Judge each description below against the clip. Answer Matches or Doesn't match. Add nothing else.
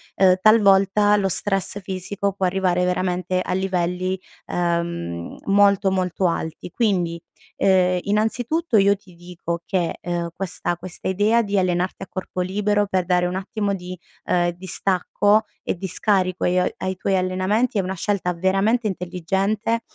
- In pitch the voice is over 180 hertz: Matches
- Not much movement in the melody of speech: Matches